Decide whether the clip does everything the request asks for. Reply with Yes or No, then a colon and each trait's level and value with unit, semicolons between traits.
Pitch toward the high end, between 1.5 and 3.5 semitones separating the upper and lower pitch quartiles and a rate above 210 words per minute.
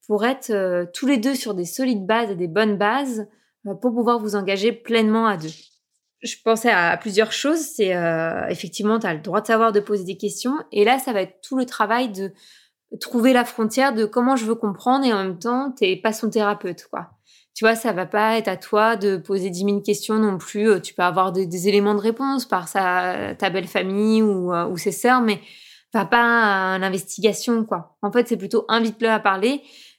Yes: high, 215 Hz; average, 3.2 semitones; fast, 220 wpm